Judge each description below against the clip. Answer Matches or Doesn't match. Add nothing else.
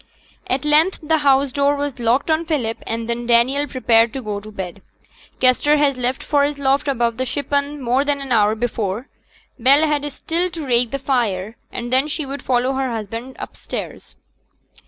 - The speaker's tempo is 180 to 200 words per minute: Matches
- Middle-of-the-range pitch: Doesn't match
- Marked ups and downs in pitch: Doesn't match